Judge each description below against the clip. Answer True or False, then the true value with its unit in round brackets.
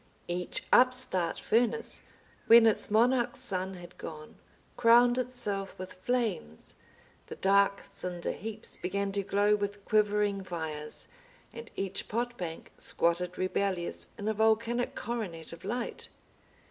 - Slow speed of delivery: True (125 wpm)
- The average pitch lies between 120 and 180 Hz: False (200 Hz)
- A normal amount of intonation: True (4.1 semitones)